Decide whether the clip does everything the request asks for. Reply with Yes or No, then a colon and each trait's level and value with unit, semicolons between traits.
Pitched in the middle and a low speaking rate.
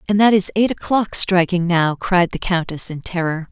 No: medium, 180 Hz; fast, 205 wpm